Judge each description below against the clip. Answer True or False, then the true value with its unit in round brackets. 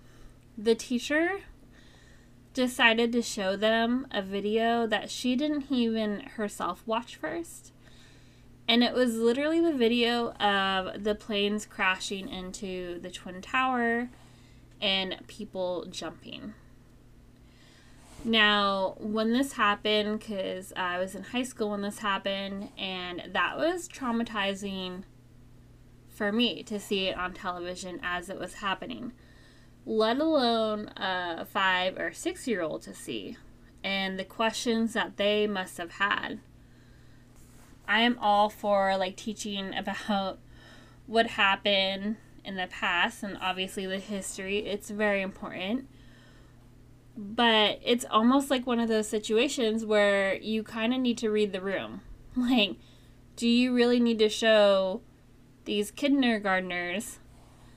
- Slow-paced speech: True (125 wpm)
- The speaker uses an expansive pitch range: False (3.8 semitones)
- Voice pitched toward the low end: False (205 Hz)